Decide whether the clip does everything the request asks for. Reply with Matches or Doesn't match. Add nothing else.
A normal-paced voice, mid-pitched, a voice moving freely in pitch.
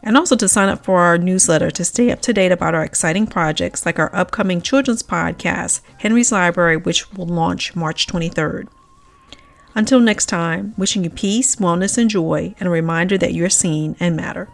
Doesn't match